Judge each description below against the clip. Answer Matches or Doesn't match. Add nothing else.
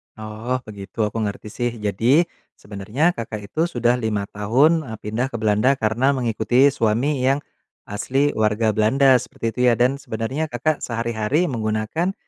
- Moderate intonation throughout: Matches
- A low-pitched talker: Matches